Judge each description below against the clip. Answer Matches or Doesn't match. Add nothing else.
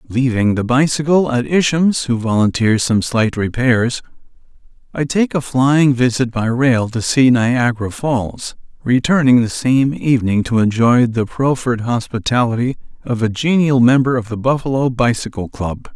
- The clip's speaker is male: Matches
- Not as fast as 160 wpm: Matches